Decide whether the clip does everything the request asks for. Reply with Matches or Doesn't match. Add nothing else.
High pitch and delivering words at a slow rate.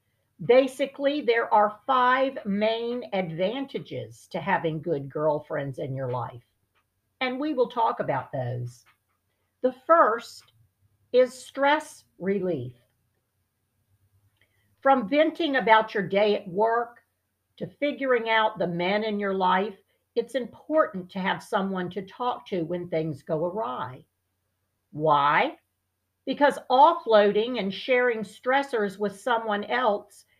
Matches